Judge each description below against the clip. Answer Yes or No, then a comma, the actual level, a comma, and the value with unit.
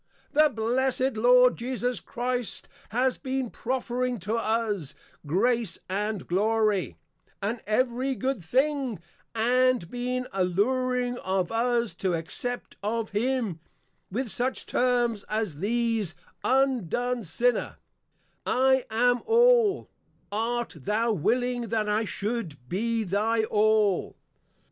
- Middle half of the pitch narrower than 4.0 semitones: Yes, average, 3.2 semitones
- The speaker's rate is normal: No, slow, 110 wpm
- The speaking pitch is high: Yes, high, 235 Hz